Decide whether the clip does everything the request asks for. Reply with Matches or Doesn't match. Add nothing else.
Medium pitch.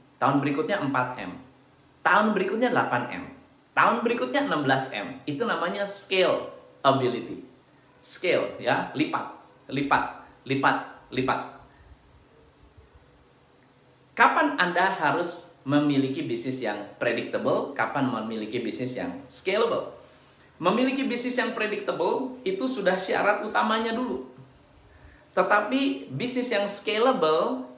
Matches